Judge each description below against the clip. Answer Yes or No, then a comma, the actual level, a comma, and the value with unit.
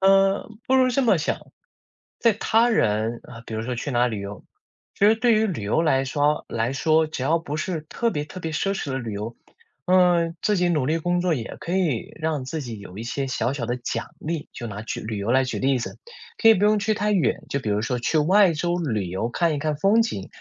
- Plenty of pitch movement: Yes, wide, 7.6 semitones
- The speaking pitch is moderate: Yes, medium, 155 Hz